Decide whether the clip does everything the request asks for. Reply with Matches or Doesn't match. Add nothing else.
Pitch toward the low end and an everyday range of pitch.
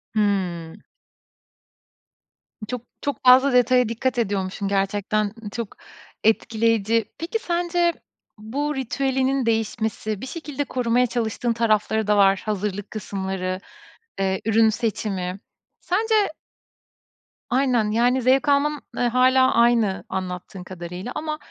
Doesn't match